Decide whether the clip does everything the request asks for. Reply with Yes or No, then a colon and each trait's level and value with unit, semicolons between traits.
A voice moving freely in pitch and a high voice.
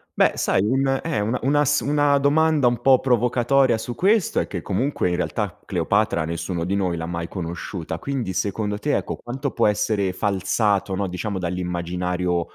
No: wide, 6.8 semitones; low, 105 Hz